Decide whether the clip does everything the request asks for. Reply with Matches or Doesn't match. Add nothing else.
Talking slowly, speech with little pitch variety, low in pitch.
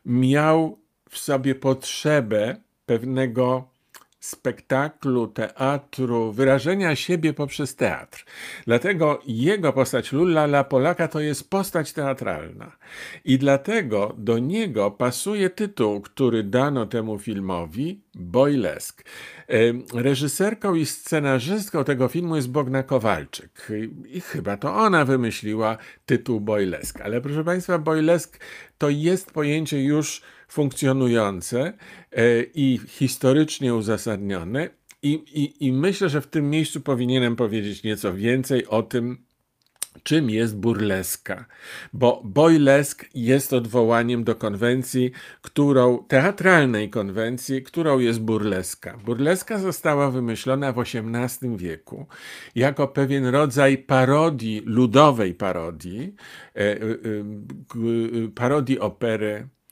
Doesn't match